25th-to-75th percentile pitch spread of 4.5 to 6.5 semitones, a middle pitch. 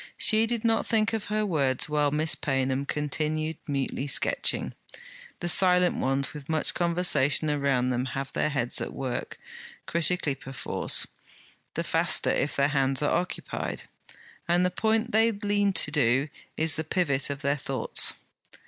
Yes: average, 4.8 semitones; medium, 150 Hz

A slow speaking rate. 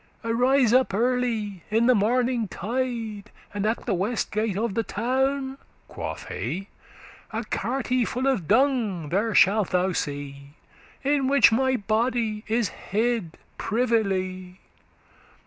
Yes: slow, 130 wpm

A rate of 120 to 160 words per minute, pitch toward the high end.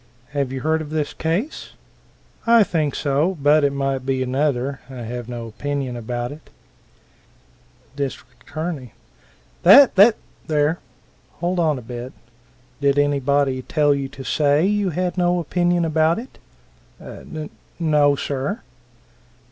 No: average, 140 wpm; medium, 145 Hz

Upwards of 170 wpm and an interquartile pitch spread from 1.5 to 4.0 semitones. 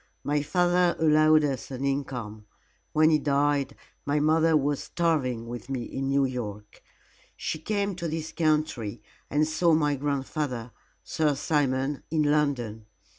No: average, 140 wpm; average, 3.1 semitones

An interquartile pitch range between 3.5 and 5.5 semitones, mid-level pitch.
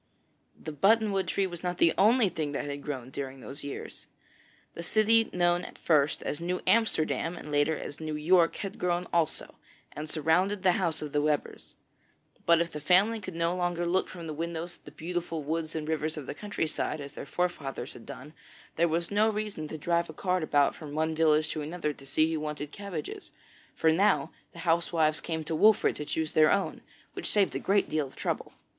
No: average, 2.9 semitones; medium, 165 Hz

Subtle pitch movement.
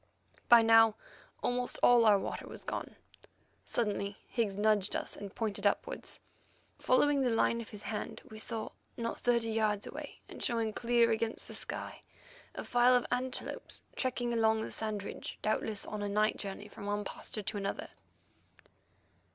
Yes: narrow, 2.2 semitones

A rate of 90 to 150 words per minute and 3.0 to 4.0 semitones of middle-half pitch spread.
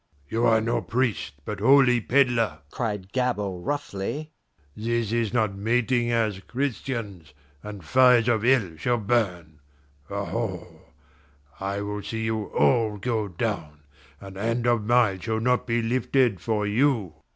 Yes: average, 140 wpm; average, 3.3 semitones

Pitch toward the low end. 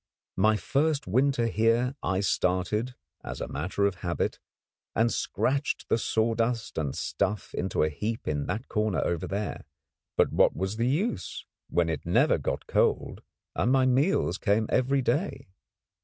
Yes: low, 110 Hz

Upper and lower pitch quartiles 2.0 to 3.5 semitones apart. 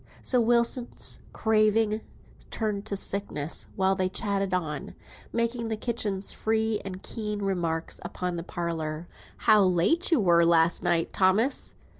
No: average, 4.2 semitones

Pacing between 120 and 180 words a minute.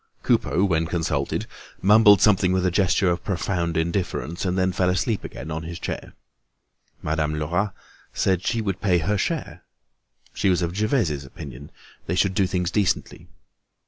Yes: average, 165 wpm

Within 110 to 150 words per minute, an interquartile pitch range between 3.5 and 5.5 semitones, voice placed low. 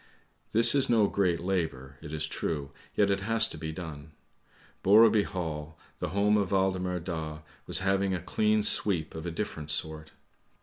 No: average, 170 wpm; average, 4.4 semitones; very low, 90 Hz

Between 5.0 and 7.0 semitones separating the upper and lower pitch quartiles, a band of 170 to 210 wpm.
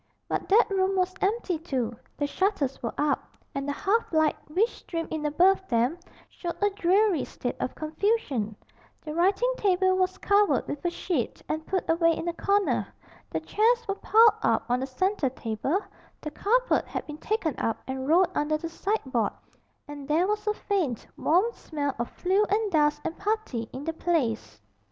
Yes: wide, 5.6 semitones; average, 180 wpm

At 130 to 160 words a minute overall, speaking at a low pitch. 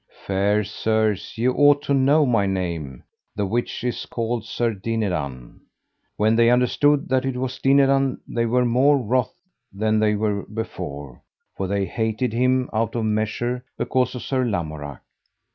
Yes: average, 155 wpm; low, 115 Hz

